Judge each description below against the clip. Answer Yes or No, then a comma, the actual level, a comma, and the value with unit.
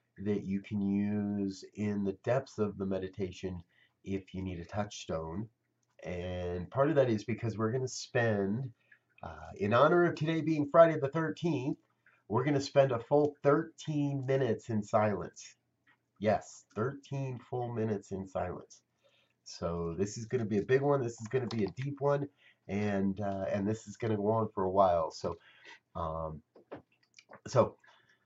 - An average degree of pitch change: No, wide, 5.8 semitones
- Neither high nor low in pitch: No, low, 110 Hz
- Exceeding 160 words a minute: Yes, average, 175 wpm